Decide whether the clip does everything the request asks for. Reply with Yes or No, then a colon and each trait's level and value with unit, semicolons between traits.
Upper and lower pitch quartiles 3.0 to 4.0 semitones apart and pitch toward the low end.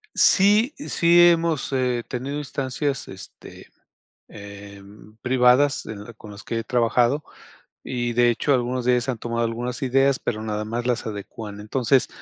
Yes: average, 3.4 semitones; low, 125 Hz